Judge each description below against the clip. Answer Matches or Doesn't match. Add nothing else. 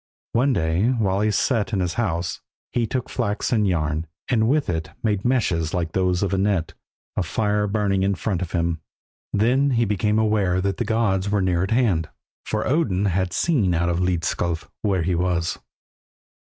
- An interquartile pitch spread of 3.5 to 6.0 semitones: Matches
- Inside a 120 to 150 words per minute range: Doesn't match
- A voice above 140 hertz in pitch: Doesn't match